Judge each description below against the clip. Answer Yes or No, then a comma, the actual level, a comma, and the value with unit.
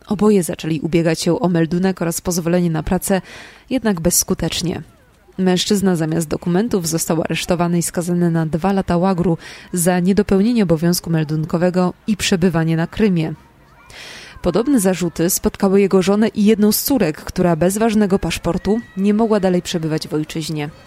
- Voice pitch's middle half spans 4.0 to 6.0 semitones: No, average, 3.0 semitones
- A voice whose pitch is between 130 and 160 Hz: No, medium, 180 Hz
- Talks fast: No, average, 145 wpm